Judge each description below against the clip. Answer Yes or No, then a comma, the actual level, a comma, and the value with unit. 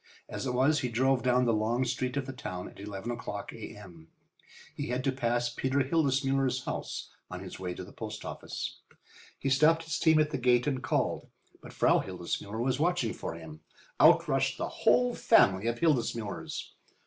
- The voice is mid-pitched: No, low, 125 Hz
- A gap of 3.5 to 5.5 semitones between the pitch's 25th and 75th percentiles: Yes, average, 4.1 semitones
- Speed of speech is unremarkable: Yes, average, 185 wpm